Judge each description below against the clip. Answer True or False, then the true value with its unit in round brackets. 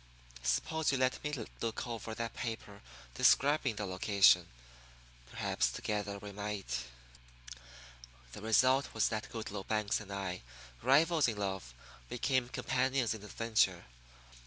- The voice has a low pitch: True (110 Hz)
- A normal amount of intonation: True (4.3 semitones)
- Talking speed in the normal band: False (130 wpm)